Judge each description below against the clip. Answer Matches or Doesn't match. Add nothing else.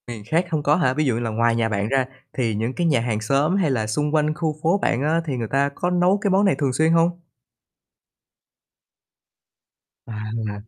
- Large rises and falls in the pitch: Matches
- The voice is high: Doesn't match